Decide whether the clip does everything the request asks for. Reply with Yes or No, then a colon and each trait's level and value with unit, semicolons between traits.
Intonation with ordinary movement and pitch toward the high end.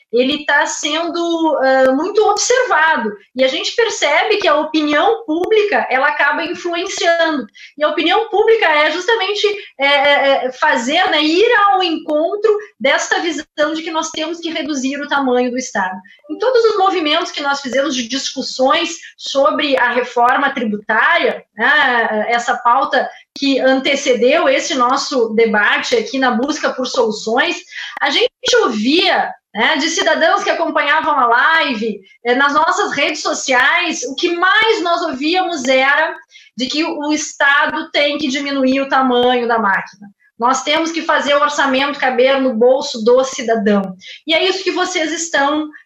Yes: average, 4.4 semitones; very high, 300 Hz